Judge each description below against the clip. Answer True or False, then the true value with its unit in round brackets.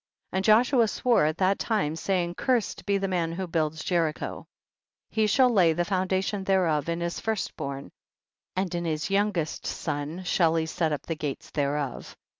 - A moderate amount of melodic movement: True (3.8 semitones)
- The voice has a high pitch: False (175 Hz)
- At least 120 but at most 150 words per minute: False (180 wpm)